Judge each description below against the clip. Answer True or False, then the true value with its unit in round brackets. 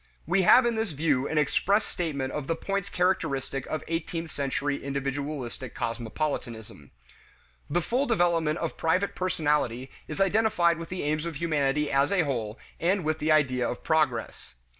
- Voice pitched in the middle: True (155 Hz)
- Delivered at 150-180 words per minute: True (160 wpm)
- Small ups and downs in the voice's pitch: False (4.3 semitones)